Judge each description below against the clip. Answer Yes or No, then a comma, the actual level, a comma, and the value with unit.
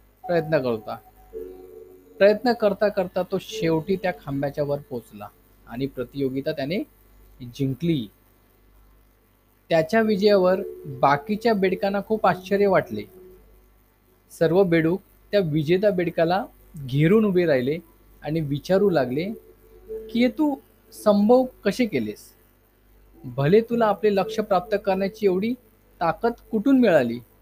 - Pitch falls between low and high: Yes, medium, 170 Hz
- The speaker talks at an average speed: Yes, average, 105 wpm